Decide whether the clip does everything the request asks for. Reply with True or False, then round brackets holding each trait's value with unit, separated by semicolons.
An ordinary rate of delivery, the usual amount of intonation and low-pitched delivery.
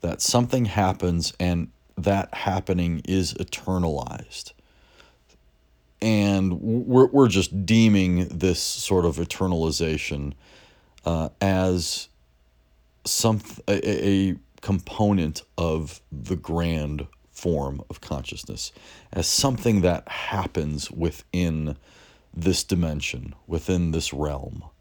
False (95 wpm; 4.4 semitones; 85 Hz)